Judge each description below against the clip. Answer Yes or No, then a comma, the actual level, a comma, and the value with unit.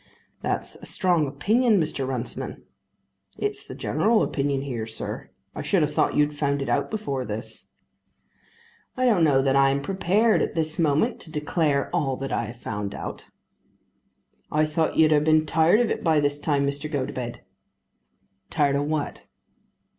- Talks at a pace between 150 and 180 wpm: Yes, average, 170 wpm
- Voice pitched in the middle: Yes, medium, 150 Hz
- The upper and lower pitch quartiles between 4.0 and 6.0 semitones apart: No, average, 3.2 semitones